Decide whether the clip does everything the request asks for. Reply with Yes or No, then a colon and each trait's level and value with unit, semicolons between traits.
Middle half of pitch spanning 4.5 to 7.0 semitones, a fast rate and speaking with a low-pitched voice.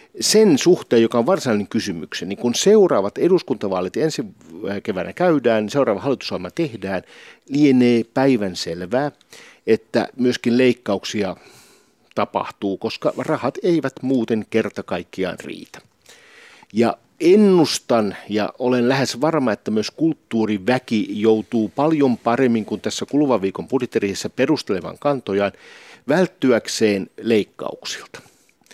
No: average, 5.3 semitones; average, 105 wpm; low, 125 Hz